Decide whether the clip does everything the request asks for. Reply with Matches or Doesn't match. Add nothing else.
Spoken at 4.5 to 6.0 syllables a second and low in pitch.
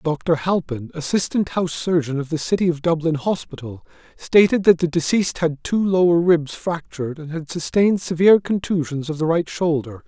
Doesn't match